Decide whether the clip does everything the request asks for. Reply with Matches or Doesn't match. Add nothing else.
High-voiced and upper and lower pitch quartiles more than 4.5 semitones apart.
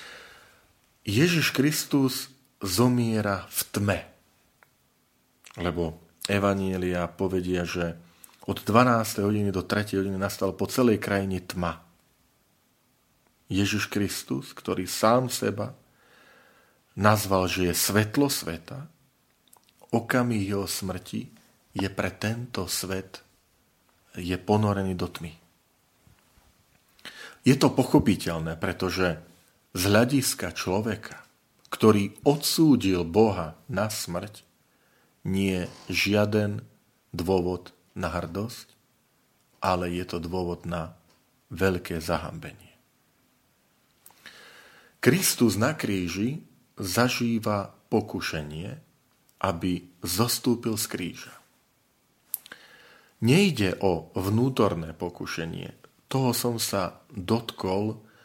Doesn't match